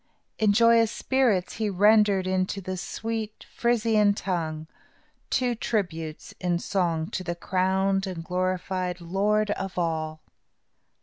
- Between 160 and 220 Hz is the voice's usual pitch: Yes, high, 190 Hz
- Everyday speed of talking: No, slow, 120 wpm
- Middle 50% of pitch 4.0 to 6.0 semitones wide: No, average, 3.1 semitones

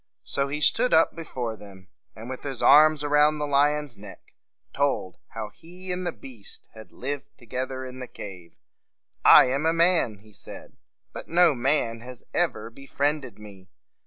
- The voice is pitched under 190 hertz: Yes, low, 135 Hz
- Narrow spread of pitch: No, average, 4.9 semitones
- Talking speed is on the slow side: No, average, 165 wpm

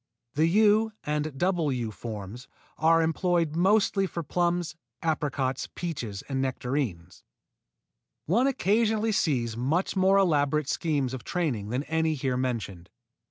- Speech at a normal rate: No, slow, 125 wpm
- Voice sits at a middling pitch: Yes, medium, 155 Hz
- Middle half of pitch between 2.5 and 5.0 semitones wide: No, wide, 5.6 semitones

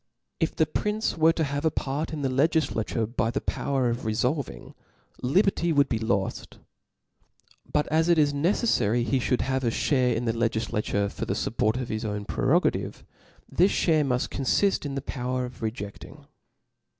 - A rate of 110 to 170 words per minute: No, average, 180 wpm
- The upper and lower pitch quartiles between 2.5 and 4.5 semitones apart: No, average, 5.2 semitones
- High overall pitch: No, low, 130 Hz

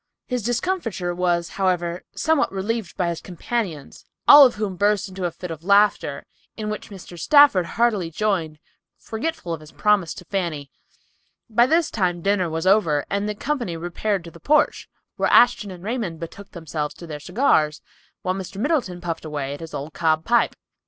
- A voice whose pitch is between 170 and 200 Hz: Yes, medium, 185 Hz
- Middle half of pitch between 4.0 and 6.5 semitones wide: Yes, average, 4.4 semitones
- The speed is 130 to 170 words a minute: No, average, 180 wpm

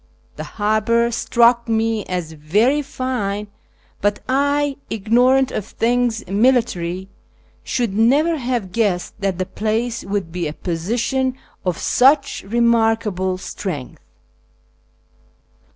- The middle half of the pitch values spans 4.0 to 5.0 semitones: Yes, average, 4.3 semitones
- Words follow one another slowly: Yes, slow, 105 wpm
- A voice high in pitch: Yes, high, 225 Hz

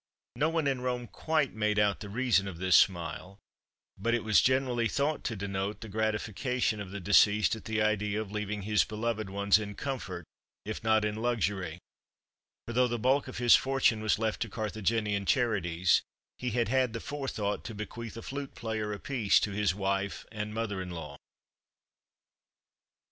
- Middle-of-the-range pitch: No, low, 110 Hz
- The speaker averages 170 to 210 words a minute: Yes, average, 175 wpm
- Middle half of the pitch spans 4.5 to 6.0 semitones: No, average, 2.9 semitones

